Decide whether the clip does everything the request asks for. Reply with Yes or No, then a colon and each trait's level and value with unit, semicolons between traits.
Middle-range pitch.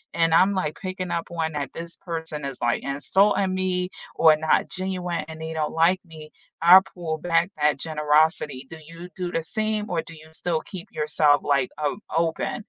Yes: medium, 165 Hz